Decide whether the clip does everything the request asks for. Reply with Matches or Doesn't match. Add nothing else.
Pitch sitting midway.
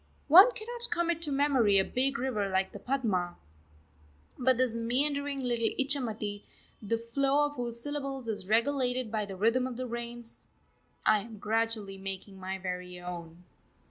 Doesn't match